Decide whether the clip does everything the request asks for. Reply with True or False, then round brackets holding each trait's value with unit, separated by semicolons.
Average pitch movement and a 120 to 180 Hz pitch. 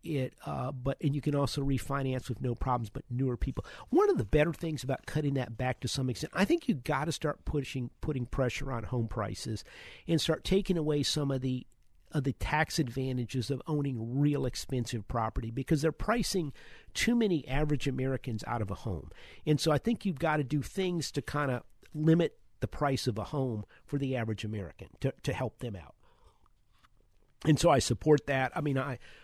True (3.6 semitones; 135 Hz)